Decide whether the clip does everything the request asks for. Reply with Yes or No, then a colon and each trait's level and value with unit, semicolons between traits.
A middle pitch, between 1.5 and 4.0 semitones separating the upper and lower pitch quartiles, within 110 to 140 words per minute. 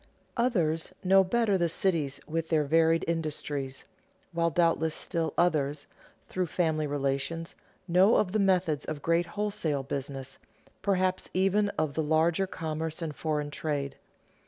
Yes: medium, 165 Hz; average, 3.4 semitones; slow, 135 wpm